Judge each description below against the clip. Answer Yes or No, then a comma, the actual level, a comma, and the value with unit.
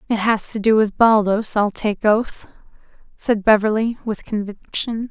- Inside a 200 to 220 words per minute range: No, average, 155 wpm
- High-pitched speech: Yes, high, 215 Hz